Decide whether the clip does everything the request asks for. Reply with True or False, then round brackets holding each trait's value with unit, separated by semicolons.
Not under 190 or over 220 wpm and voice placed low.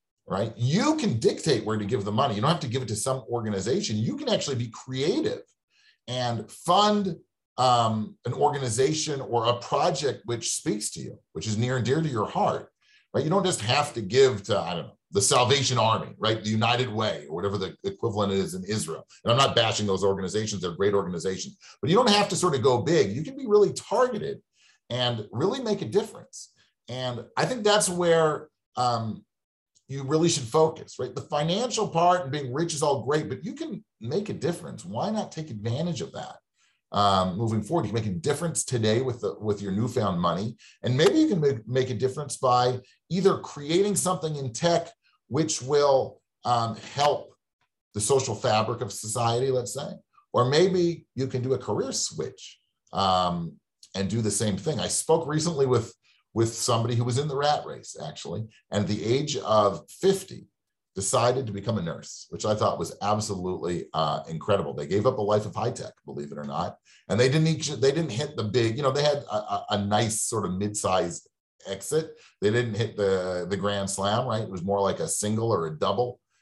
True (205 wpm; 125 Hz)